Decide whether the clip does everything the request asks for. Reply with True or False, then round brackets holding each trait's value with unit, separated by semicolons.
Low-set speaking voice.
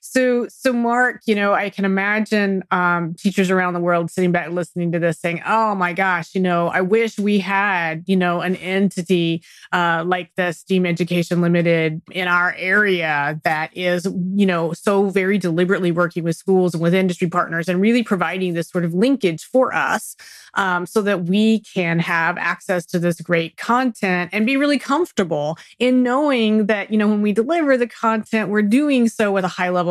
False (185 Hz)